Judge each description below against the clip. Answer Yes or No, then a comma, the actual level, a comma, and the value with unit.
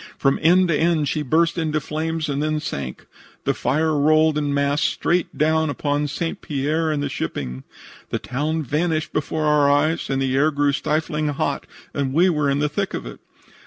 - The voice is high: No, medium, 150 Hz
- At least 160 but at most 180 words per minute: No, average, 195 wpm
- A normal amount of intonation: No, narrow, 1.9 semitones